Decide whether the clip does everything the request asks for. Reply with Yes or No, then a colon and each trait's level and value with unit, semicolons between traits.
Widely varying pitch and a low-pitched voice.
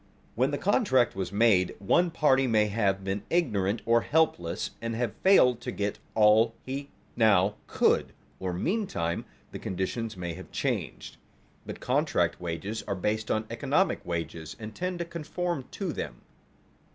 Yes: wide, 5.9 semitones; low, 110 Hz